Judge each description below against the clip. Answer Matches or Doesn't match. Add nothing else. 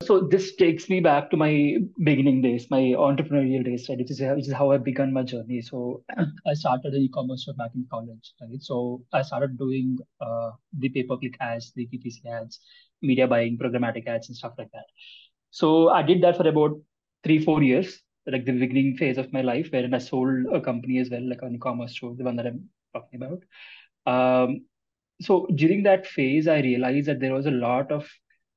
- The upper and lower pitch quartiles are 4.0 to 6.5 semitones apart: Doesn't match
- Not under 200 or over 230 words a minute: Matches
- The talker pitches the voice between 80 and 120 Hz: Doesn't match